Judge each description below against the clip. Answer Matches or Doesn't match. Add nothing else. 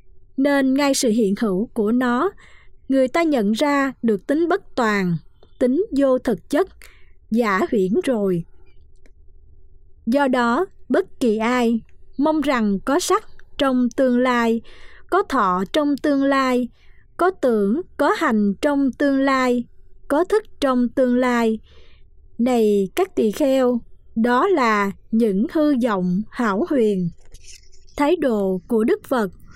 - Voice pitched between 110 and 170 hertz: Doesn't match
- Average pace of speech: Doesn't match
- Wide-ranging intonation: Doesn't match